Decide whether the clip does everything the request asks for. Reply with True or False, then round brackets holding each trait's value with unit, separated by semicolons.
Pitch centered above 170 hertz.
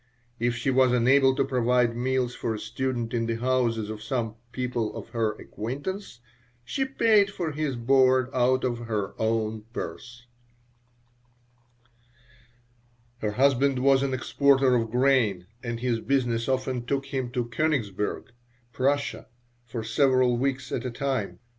False (125 Hz)